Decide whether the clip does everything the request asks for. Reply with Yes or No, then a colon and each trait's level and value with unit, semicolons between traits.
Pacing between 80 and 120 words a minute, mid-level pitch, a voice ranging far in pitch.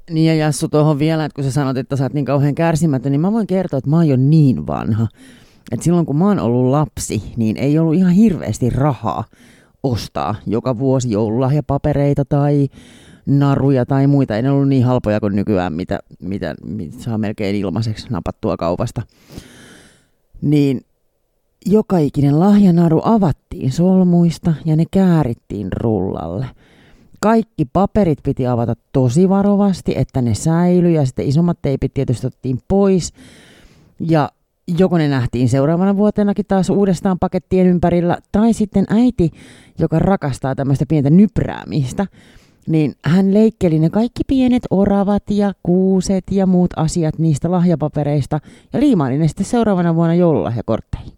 No: average, 150 wpm; medium, 150 Hz; wide, 5.9 semitones